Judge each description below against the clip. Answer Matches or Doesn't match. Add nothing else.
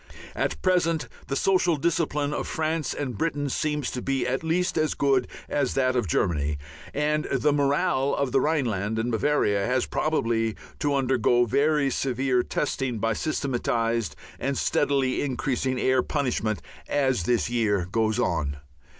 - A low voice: Matches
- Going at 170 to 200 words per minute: Doesn't match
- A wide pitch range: Doesn't match